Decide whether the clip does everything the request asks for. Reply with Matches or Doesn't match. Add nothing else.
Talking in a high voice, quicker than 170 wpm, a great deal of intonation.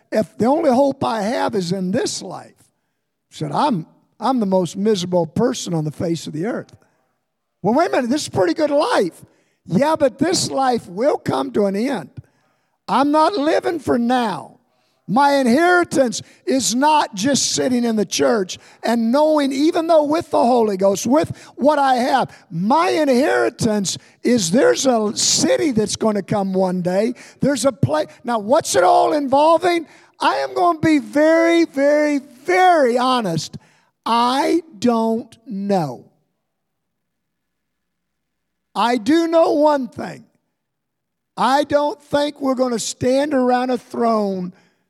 Doesn't match